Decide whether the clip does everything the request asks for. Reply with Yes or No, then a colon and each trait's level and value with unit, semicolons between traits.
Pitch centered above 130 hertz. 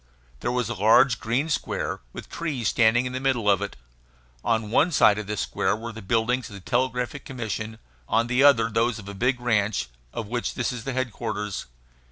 No: low, 115 Hz